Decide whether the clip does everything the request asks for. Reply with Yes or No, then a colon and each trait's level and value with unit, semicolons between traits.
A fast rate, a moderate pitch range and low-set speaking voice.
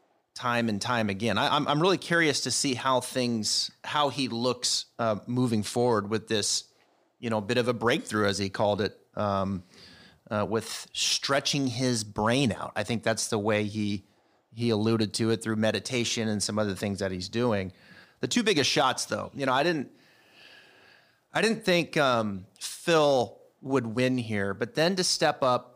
No: average, 185 wpm; average, 3.7 semitones; low, 115 Hz